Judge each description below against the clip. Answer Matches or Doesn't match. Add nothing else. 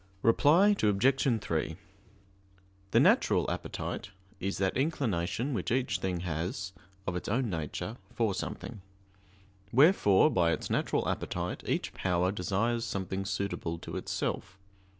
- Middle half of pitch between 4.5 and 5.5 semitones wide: Matches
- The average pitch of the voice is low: Matches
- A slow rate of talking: Matches